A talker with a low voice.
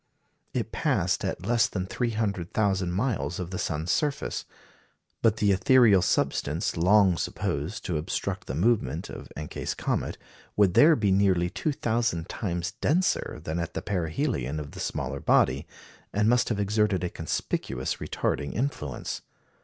Yes: very low, 95 Hz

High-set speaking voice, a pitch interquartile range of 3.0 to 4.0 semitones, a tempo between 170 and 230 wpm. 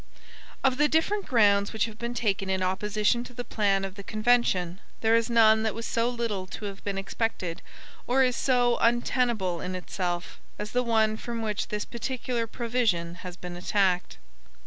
Yes: high, 220 Hz; average, 3.6 semitones; average, 180 wpm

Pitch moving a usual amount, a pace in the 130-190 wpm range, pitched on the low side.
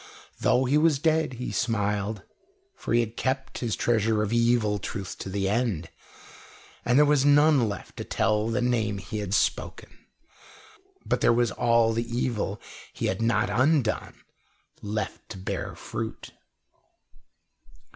Yes: average, 3.2 semitones; average, 145 wpm; low, 115 Hz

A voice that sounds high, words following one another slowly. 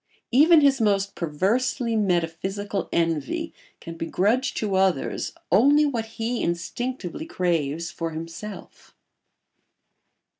Yes: high, 200 Hz; slow, 100 wpm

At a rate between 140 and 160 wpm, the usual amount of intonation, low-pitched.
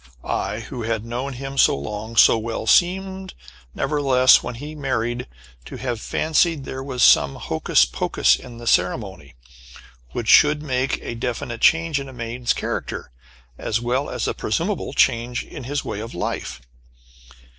Yes: average, 155 wpm; average, 3.3 semitones; low, 125 Hz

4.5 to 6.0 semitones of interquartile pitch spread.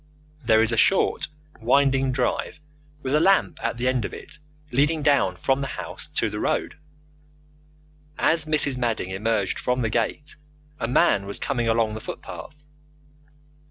No: average, 3.8 semitones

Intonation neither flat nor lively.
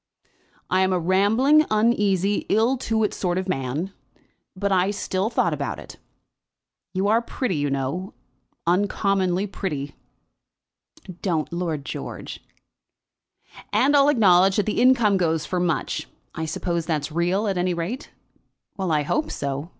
Yes: average, 3.7 semitones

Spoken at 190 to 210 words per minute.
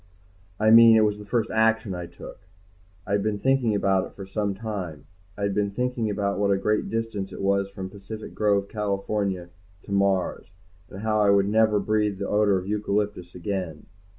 Yes: average, 195 wpm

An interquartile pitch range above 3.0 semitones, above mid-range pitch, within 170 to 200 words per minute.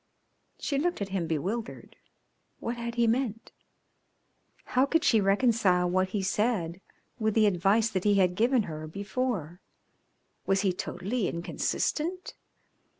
No: average, 4.2 semitones; high, 205 Hz; slow, 135 wpm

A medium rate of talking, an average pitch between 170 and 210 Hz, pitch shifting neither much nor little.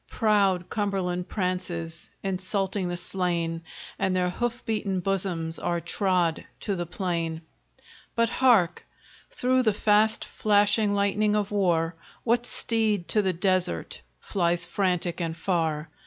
No: slow, 125 wpm; medium, 185 Hz; average, 3.1 semitones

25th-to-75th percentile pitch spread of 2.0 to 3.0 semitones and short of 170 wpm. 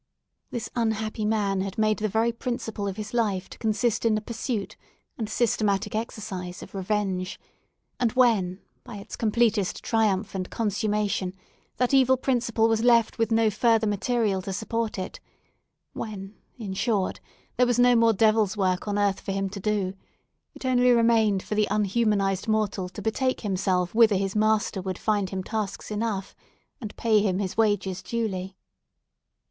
Yes: average, 2.7 semitones; average, 160 wpm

